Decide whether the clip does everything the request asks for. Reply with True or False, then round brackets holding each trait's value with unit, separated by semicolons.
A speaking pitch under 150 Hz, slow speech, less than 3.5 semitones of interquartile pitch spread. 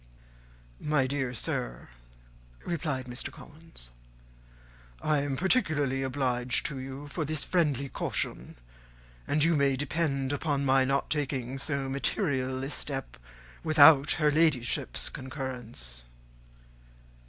True (140 Hz; 110 wpm; 2.5 semitones)